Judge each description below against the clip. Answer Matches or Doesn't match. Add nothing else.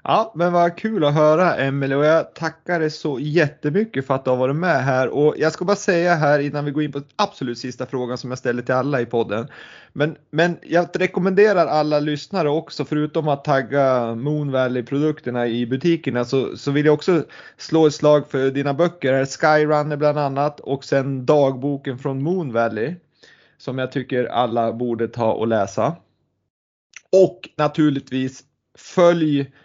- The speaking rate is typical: Matches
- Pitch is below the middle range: Doesn't match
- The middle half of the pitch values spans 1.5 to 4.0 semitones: Matches